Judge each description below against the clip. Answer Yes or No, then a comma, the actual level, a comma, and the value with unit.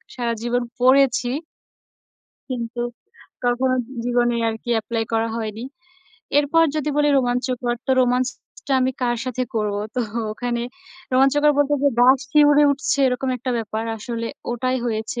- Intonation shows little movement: Yes, narrow, 1.9 semitones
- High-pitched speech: Yes, high, 245 Hz